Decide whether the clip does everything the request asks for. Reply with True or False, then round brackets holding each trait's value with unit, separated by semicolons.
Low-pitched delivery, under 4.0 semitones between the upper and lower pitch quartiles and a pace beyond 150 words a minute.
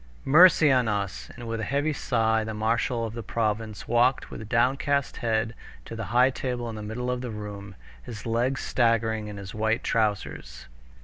True (115 Hz; 2.5 semitones; 185 wpm)